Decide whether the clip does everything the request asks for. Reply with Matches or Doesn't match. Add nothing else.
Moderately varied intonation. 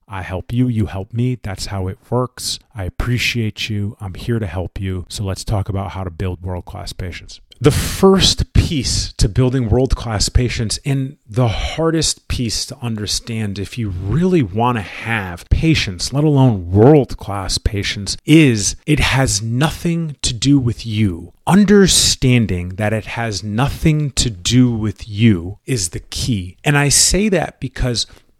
Matches